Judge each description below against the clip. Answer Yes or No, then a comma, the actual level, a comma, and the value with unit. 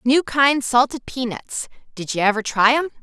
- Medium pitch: No, very high, 250 Hz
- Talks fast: No, average, 180 wpm